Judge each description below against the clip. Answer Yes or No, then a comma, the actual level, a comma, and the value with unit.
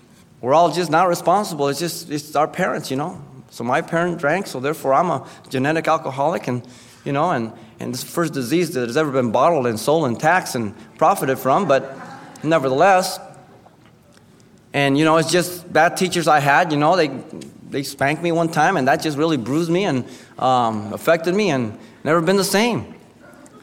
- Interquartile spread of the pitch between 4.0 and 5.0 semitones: Yes, average, 4.4 semitones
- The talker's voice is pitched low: No, medium, 155 Hz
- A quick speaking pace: No, average, 195 wpm